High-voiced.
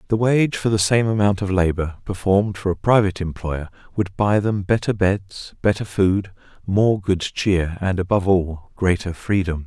No: very low, 95 Hz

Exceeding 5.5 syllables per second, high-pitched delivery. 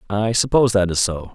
No: 6.0 syllables/s; low, 100 Hz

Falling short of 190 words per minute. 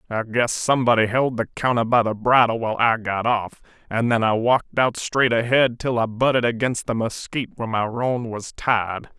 No: fast, 205 wpm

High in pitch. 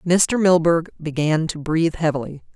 No: medium, 160 Hz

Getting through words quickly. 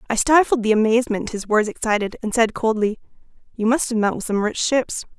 Yes: fast, 210 wpm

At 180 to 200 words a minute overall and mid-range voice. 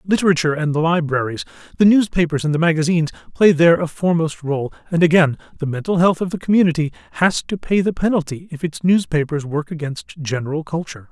Yes: average, 185 wpm; medium, 165 Hz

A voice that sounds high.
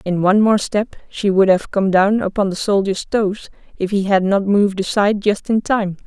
Yes: high, 200 Hz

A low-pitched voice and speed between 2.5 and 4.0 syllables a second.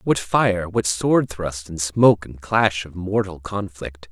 Yes: very low, 95 Hz; 3.7 syllables/s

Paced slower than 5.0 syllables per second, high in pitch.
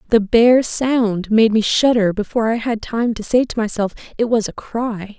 Yes: 4.7 syllables/s; high, 225 Hz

